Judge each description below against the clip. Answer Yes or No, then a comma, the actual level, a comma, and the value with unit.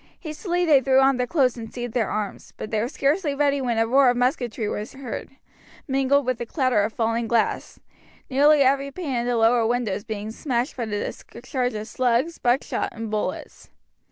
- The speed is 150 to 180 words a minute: No, average, 195 wpm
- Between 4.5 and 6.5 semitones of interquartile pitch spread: No, average, 3.3 semitones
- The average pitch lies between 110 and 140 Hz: No, high, 245 Hz